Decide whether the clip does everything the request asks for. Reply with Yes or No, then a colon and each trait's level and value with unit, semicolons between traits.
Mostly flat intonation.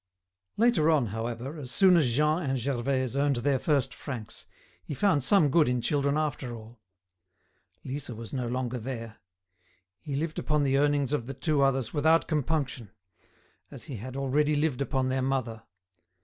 No: average, 3.2 semitones